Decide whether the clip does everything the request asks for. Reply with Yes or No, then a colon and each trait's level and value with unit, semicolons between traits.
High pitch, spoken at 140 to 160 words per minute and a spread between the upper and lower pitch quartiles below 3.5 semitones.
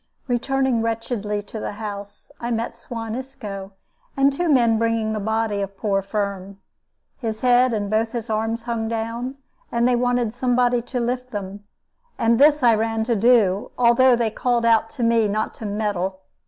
No: high, 230 Hz; average, 175 wpm; narrow, 2.5 semitones